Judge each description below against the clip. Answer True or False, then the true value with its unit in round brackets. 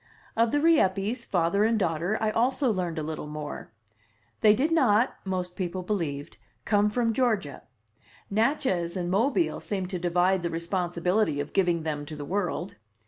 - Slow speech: False (160 wpm)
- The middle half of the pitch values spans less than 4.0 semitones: False (4.5 semitones)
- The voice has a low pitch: False (190 Hz)